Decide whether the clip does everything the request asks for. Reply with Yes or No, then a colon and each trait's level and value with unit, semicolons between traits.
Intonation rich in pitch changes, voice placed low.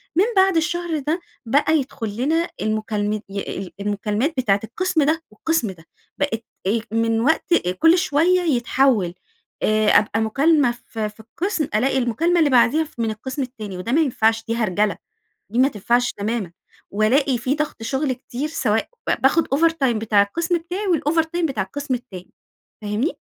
No: wide, 6.5 semitones; very high, 250 Hz